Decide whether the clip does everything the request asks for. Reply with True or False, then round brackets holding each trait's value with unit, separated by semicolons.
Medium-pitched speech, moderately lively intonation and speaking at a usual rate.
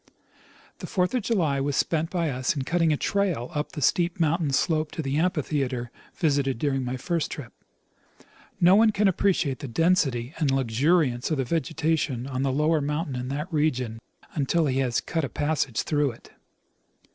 True (150 Hz; 3.8 semitones; 180 wpm)